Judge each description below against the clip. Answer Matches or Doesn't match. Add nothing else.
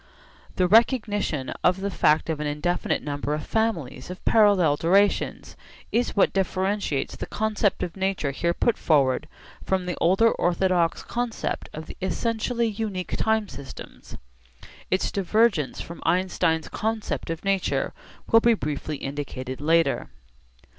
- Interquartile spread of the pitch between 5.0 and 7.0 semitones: Matches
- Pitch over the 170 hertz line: Matches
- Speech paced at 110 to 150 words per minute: Matches